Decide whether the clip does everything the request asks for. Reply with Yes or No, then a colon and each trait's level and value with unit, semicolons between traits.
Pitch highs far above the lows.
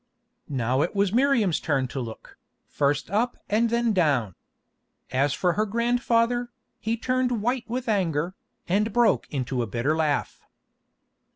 Yes: wide, 8.5 semitones